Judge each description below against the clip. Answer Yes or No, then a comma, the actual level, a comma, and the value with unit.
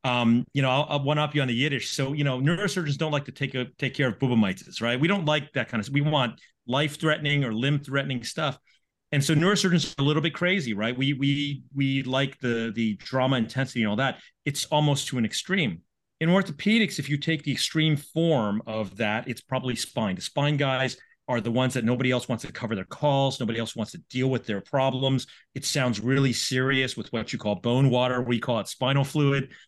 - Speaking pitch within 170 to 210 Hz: No, low, 135 Hz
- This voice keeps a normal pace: No, fast, 225 wpm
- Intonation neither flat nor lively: Yes, average, 3.1 semitones